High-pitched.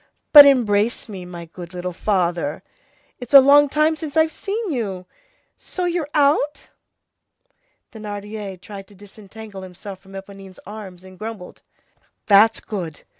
Yes: high, 205 Hz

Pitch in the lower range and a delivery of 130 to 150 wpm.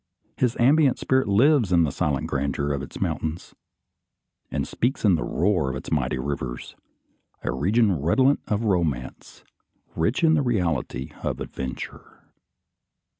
Yes: very low, 85 Hz; average, 140 wpm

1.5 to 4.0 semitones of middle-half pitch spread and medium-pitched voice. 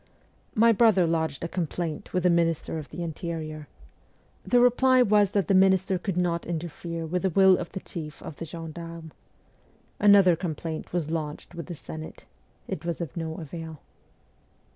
Yes: average, 2.8 semitones; medium, 170 Hz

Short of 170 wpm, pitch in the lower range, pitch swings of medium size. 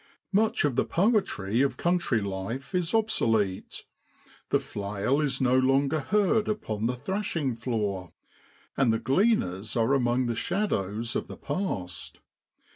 No: slow, 135 wpm; low, 130 Hz; wide, 8.8 semitones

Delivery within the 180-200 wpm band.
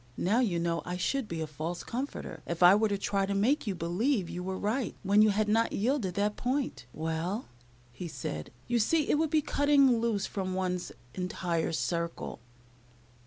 Yes: average, 190 wpm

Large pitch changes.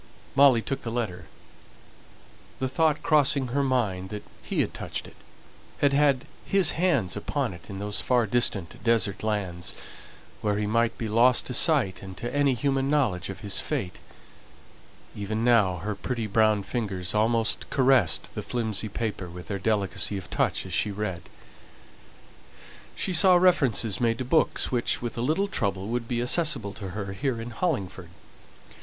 No: average, 4.9 semitones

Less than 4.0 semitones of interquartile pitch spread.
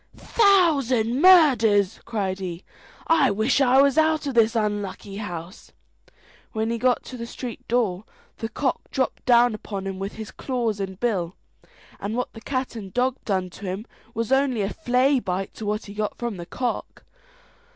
No: average, 4.3 semitones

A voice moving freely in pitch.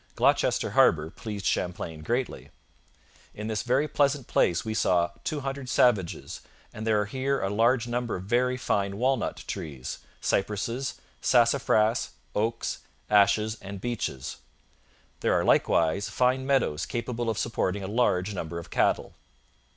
No: average, 4.4 semitones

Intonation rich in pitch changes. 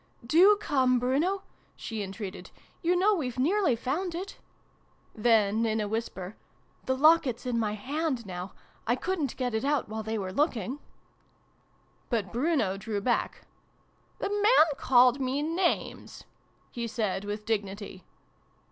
Yes: wide, 6.3 semitones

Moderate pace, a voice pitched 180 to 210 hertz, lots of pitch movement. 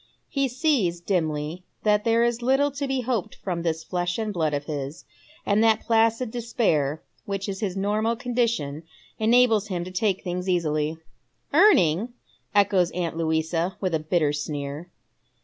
Yes: average, 155 wpm; high, 190 Hz; wide, 5.9 semitones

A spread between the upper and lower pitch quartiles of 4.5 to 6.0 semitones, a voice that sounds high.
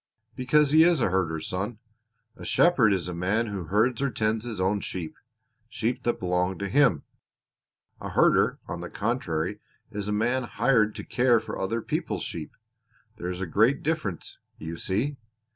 No: average, 5.0 semitones; low, 105 Hz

